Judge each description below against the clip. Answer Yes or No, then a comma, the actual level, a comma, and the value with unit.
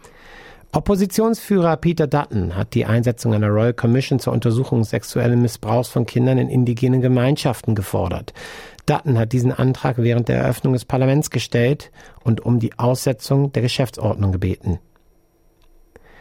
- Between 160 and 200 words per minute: No, average, 135 wpm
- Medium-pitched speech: No, low, 125 Hz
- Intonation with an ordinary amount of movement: Yes, average, 3.1 semitones